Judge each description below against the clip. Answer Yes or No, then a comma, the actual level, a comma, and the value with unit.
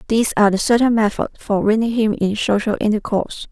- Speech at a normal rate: Yes, average, 190 wpm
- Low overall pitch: No, high, 215 Hz